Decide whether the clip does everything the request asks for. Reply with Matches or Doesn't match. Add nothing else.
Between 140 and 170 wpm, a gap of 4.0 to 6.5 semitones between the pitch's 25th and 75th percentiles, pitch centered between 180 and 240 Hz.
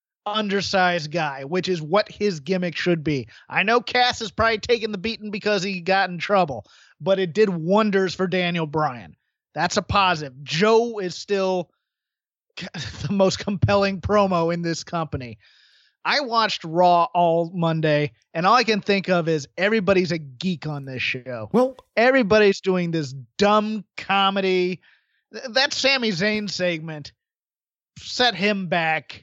Matches